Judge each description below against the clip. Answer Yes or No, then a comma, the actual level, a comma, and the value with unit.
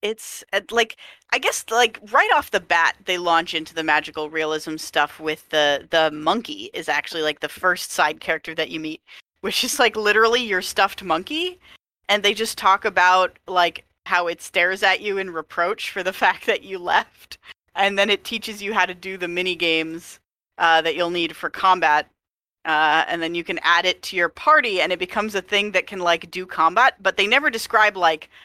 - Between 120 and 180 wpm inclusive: No, fast, 205 wpm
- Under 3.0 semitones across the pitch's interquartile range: No, average, 4.2 semitones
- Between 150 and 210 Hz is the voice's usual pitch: Yes, medium, 185 Hz